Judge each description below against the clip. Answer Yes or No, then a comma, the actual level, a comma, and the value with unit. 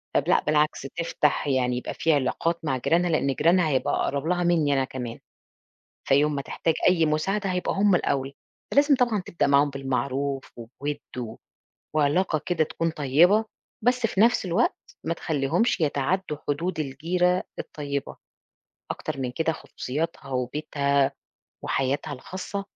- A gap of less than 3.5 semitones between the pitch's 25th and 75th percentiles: No, average, 4.4 semitones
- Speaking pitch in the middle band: Yes, medium, 150 Hz